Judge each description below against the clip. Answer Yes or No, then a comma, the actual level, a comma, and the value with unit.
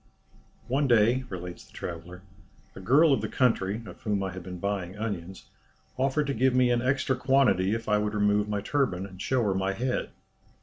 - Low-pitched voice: Yes, low, 105 Hz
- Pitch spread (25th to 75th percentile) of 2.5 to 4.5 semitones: No, average, 5.0 semitones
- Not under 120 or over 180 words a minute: No, average, 200 wpm